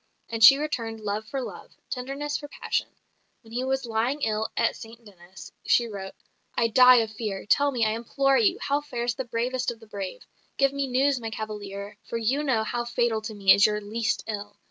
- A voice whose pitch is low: No, high, 230 Hz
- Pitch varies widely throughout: No, average, 3.5 semitones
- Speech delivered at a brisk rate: Yes, fast, 210 wpm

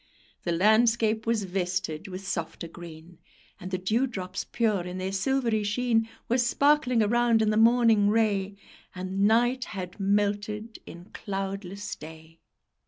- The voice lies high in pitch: Yes, high, 205 Hz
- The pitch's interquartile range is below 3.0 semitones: No, average, 3.5 semitones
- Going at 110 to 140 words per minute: Yes, slow, 135 wpm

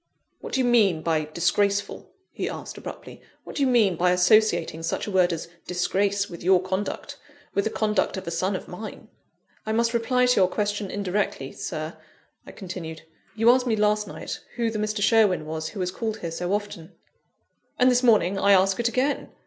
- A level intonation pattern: No, average, 3.6 semitones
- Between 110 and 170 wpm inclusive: No, average, 200 wpm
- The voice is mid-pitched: No, high, 200 Hz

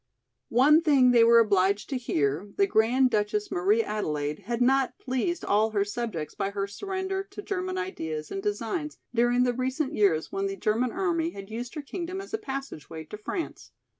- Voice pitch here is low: No, high, 245 Hz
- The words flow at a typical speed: Yes, average, 185 wpm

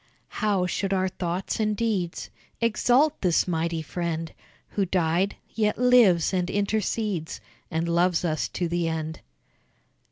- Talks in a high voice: No, medium, 180 Hz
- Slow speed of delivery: Yes, slow, 130 wpm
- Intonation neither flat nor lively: Yes, average, 3.8 semitones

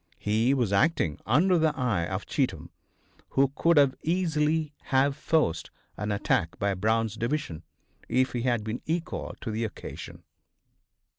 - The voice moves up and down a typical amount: No, wide, 6.1 semitones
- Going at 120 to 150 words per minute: Yes, average, 140 wpm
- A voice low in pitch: Yes, low, 125 Hz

